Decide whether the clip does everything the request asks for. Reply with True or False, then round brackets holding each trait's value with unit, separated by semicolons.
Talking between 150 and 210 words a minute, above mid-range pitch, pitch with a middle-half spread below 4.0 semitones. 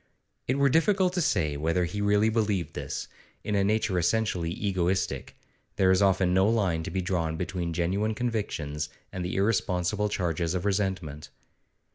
False (160 wpm; 95 Hz; 3.4 semitones)